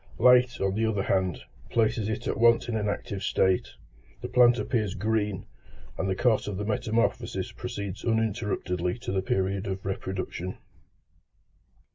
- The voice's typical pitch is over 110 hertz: No, low, 105 Hz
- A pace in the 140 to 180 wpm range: Yes, average, 150 wpm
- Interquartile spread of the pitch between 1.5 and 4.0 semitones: Yes, average, 2.9 semitones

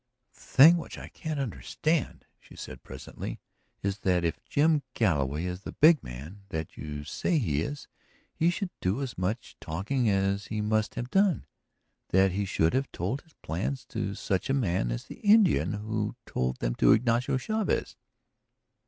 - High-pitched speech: No, low, 105 Hz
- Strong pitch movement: Yes, wide, 7.8 semitones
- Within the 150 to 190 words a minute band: Yes, average, 170 wpm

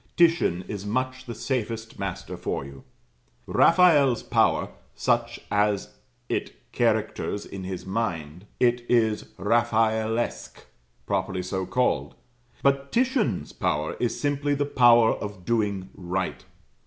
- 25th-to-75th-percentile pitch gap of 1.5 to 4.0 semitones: No, average, 5.1 semitones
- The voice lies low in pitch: Yes, low, 110 Hz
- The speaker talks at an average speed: No, slow, 115 wpm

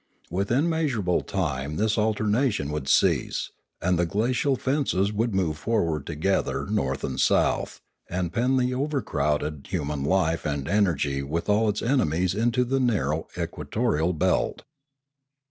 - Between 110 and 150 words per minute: Yes, average, 140 wpm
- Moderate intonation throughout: No, wide, 7.2 semitones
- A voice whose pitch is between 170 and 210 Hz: No, very low, 95 Hz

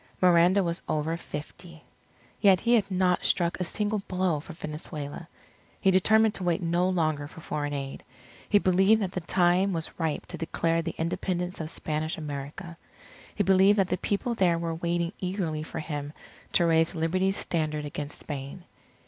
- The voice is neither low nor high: Yes, medium, 170 Hz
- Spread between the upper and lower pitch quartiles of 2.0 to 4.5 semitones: Yes, average, 3.0 semitones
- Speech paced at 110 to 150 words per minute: No, average, 170 wpm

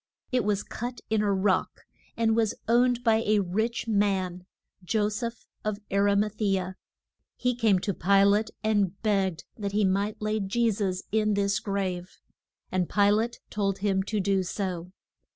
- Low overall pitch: No, high, 205 Hz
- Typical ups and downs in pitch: No, narrow, 2.1 semitones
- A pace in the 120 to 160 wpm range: No, average, 175 wpm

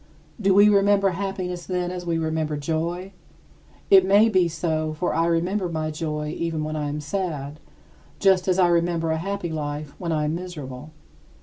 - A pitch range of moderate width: Yes, average, 3.0 semitones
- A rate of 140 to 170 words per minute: No, average, 180 wpm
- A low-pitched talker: No, medium, 170 Hz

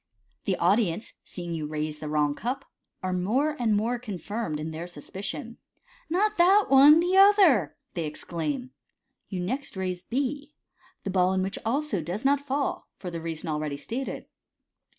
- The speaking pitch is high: Yes, high, 205 Hz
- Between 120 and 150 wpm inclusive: No, average, 170 wpm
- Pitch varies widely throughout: Yes, wide, 8.6 semitones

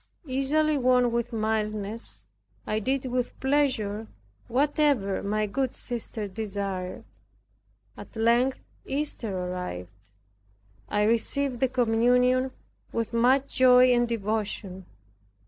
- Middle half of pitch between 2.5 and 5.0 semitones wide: Yes, average, 3.7 semitones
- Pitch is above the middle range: Yes, high, 235 Hz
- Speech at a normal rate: No, slow, 100 wpm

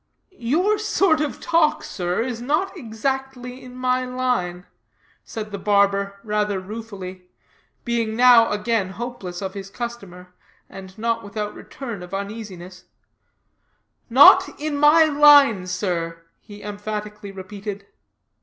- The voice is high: Yes, high, 215 Hz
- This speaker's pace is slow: Yes, slow, 120 wpm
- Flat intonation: No, average, 4.5 semitones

